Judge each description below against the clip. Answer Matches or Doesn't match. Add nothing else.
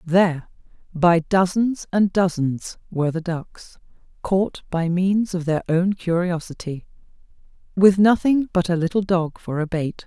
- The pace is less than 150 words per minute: Matches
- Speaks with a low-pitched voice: Doesn't match